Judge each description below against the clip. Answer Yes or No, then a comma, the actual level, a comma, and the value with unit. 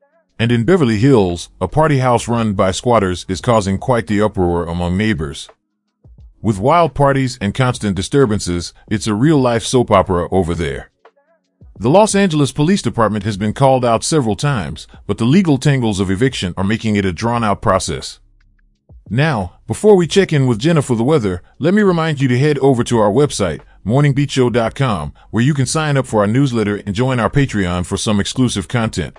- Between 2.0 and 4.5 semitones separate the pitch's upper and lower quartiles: No, wide, 5.5 semitones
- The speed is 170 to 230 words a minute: Yes, average, 190 wpm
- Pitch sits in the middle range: No, low, 115 Hz